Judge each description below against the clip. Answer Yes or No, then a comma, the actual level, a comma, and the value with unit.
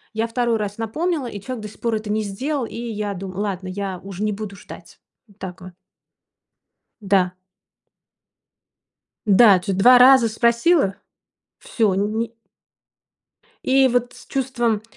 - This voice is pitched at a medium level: No, high, 215 Hz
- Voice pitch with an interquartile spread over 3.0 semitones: Yes, average, 3.4 semitones